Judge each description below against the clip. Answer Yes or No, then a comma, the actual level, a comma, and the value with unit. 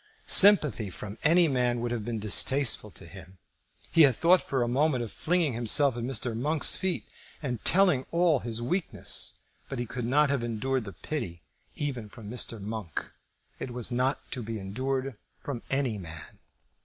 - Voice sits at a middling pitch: No, low, 125 Hz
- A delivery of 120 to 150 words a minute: No, average, 170 wpm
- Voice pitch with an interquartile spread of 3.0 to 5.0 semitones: Yes, average, 4.3 semitones